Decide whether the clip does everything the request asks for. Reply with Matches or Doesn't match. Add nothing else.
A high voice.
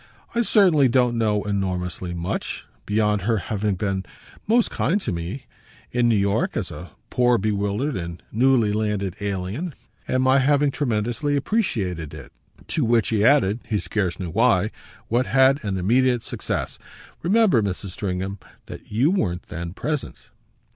Doesn't match